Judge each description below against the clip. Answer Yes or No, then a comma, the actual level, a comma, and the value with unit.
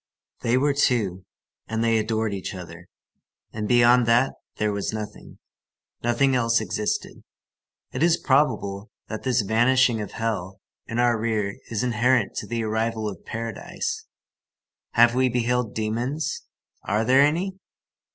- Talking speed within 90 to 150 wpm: Yes, average, 140 wpm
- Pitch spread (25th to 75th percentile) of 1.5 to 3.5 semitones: Yes, narrow, 2.6 semitones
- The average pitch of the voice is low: Yes, low, 115 Hz